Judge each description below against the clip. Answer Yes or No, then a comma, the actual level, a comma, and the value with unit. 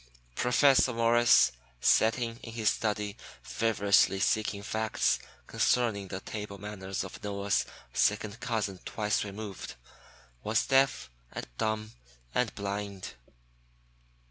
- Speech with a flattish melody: Yes, narrow, 2.3 semitones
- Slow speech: Yes, slow, 105 wpm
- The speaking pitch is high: No, low, 105 Hz